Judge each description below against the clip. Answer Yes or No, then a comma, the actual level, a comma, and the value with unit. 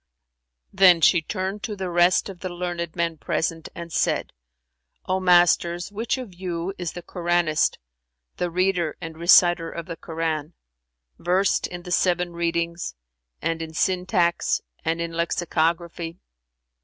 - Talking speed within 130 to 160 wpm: Yes, average, 140 wpm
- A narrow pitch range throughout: Yes, narrow, 1.4 semitones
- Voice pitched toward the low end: No, medium, 175 Hz